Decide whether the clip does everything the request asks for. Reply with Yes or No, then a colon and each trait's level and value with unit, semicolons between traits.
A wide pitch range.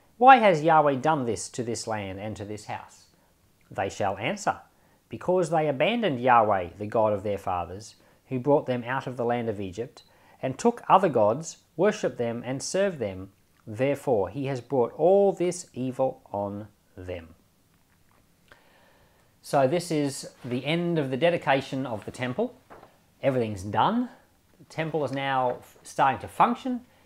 Yes: wide, 7.0 semitones